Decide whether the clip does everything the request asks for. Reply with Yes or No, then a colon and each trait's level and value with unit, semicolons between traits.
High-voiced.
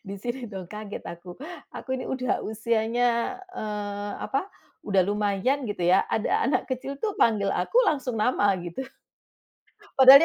Yes: high, 220 Hz